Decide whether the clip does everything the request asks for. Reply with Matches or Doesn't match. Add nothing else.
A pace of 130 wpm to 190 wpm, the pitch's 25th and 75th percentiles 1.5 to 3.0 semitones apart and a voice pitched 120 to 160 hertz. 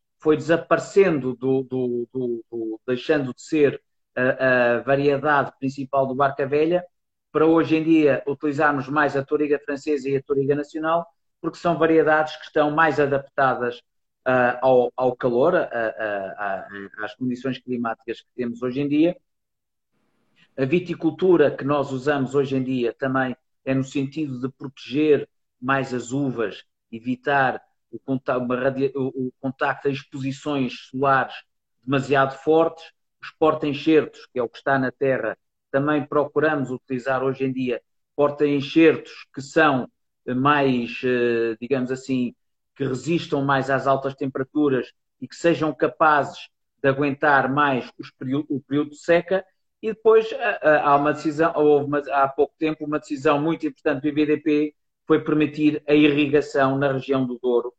Matches